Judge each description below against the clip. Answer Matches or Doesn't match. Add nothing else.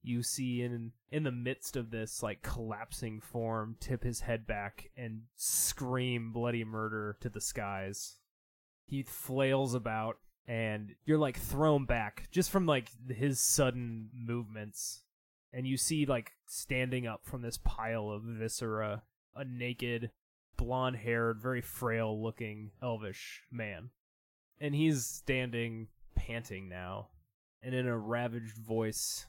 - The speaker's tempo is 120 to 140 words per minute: Matches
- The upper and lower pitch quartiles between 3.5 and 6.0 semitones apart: Doesn't match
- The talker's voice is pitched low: Matches